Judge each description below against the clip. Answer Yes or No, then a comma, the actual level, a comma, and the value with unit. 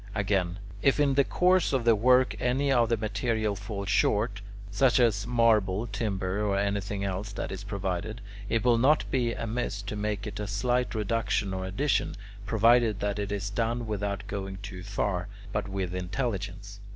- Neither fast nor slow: Yes, average, 170 wpm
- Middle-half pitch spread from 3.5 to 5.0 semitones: No, average, 2.9 semitones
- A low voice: Yes, low, 105 Hz